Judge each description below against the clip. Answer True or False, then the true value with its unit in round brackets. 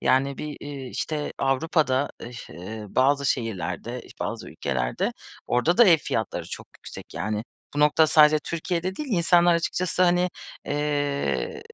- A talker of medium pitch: True (145 Hz)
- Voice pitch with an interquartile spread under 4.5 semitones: False (5.3 semitones)